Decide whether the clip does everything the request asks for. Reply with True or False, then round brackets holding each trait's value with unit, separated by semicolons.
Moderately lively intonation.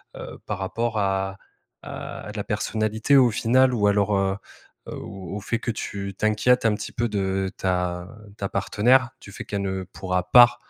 True (3.0 semitones)